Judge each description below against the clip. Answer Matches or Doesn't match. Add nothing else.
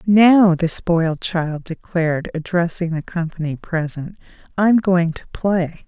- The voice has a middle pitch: Matches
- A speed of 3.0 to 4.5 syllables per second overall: Matches